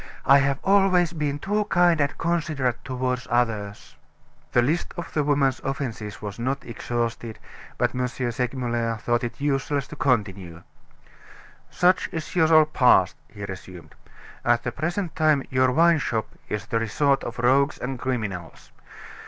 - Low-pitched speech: Yes, low, 130 Hz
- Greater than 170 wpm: No, average, 145 wpm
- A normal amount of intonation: Yes, average, 4.4 semitones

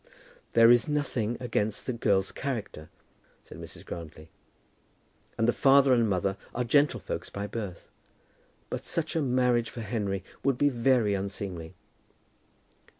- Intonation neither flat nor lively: Yes, average, 4.4 semitones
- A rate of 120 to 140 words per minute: Yes, slow, 135 wpm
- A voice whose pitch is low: Yes, low, 115 Hz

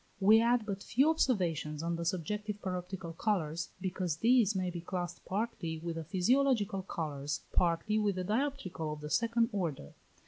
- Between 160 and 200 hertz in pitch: Yes, medium, 185 Hz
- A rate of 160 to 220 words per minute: Yes, average, 165 wpm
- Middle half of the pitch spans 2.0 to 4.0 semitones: No, average, 4.5 semitones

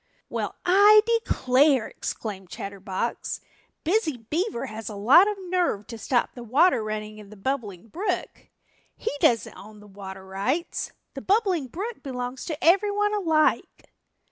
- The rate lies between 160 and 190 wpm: No, average, 145 wpm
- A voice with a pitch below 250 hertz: No, very high, 255 Hz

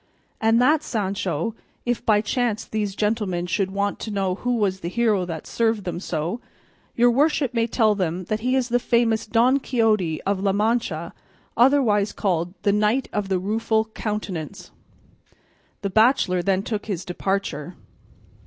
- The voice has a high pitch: Yes, high, 210 Hz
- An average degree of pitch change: Yes, average, 3.5 semitones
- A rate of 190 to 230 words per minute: No, average, 160 wpm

